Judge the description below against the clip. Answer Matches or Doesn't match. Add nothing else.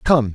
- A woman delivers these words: Doesn't match